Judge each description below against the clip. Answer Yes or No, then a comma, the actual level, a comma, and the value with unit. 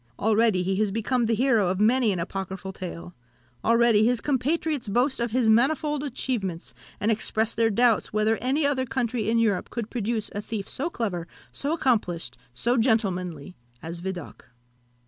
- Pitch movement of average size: Yes, average, 4.4 semitones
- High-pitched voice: Yes, high, 225 Hz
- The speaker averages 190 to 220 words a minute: No, average, 165 wpm